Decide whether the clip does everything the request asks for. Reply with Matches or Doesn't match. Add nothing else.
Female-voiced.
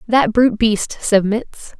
Matches